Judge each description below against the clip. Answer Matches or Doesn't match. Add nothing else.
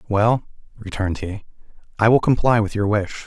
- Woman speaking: Doesn't match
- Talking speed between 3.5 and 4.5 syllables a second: Doesn't match